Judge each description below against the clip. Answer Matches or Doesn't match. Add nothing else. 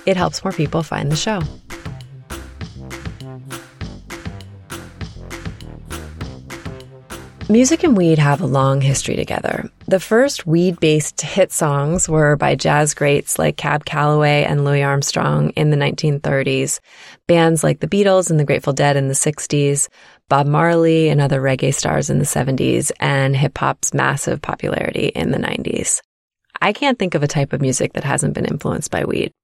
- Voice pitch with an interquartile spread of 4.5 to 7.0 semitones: Doesn't match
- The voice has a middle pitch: Matches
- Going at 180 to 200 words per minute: Doesn't match